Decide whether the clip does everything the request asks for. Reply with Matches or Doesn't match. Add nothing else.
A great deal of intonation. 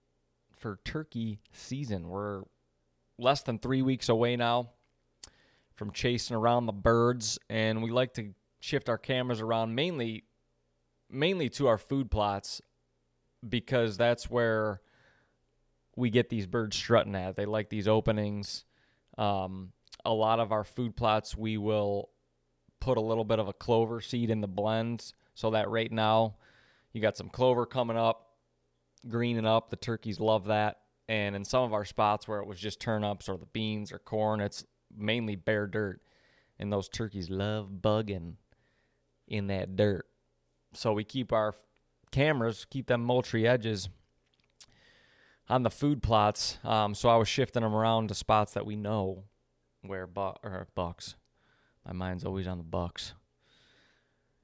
Doesn't match